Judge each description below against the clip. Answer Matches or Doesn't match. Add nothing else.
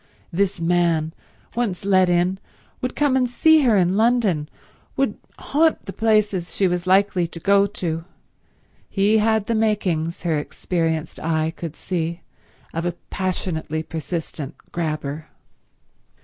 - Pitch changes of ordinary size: Matches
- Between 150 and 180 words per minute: Doesn't match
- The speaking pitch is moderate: Matches